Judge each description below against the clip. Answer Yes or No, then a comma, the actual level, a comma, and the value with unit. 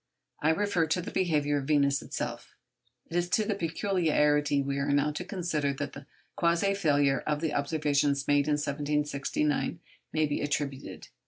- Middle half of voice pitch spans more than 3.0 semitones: No, narrow, 2.6 semitones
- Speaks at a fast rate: No, average, 165 wpm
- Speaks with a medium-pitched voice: Yes, medium, 150 Hz